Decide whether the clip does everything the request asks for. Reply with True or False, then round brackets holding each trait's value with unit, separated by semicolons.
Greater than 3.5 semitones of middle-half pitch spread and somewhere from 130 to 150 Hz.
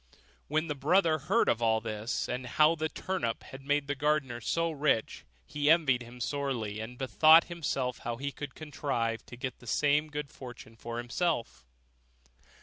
True (4.3 semitones; 140 Hz)